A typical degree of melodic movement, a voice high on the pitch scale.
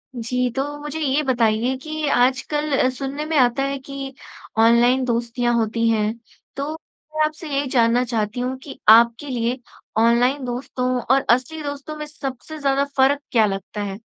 Yes: average, 3.3 semitones; very high, 260 Hz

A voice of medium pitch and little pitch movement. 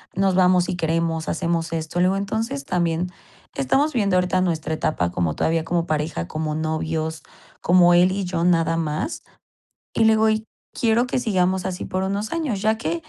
No: medium, 180 Hz; average, 3.6 semitones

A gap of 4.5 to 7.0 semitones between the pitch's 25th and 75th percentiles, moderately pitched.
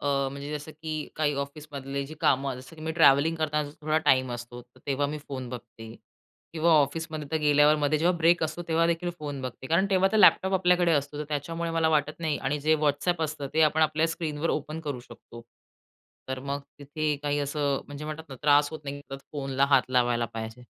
No: narrow, 2.4 semitones; medium, 150 Hz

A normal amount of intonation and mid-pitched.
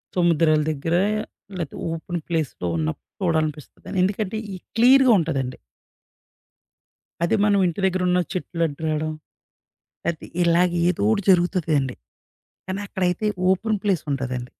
Yes: average, 3.5 semitones; medium, 170 Hz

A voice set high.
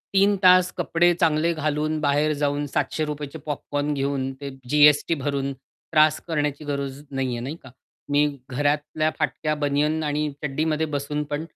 No: medium, 150 Hz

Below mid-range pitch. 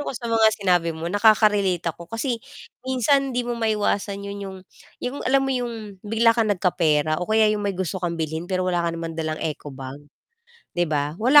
No: high, 200 Hz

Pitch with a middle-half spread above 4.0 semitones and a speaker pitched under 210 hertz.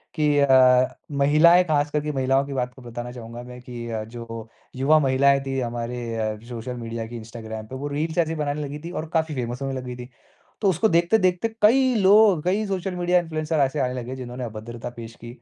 Yes: average, 4.7 semitones; low, 135 Hz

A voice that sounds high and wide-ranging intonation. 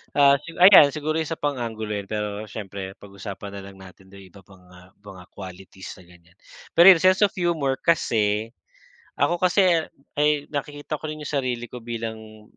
No: low, 115 Hz; wide, 7.3 semitones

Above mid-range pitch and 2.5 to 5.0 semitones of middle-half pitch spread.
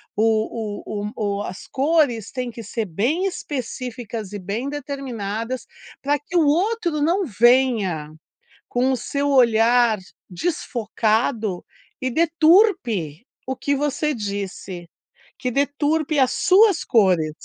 No: high, 245 Hz; wide, 5.5 semitones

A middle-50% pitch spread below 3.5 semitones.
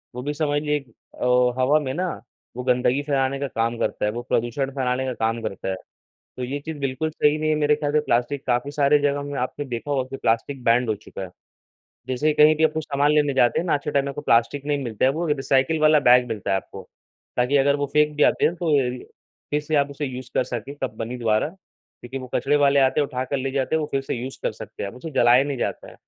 Yes: average, 2.8 semitones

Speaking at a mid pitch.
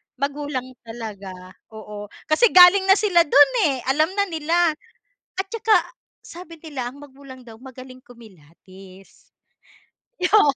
No: very high, 275 Hz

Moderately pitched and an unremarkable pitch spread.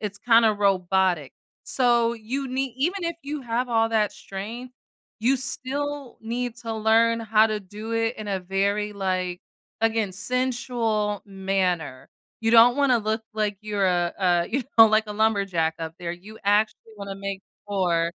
No: high, 215 Hz; average, 3.5 semitones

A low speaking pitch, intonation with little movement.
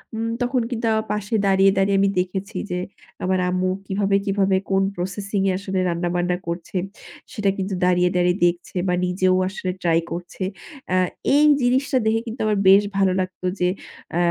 No: high, 190 Hz; narrow, 2.3 semitones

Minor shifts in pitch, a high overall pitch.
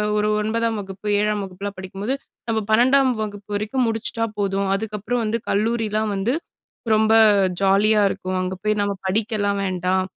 Yes: narrow, 2.1 semitones; high, 210 Hz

